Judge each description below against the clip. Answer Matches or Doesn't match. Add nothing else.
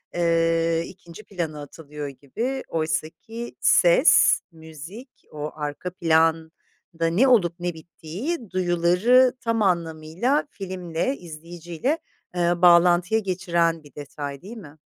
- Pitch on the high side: Doesn't match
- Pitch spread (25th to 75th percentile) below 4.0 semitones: Matches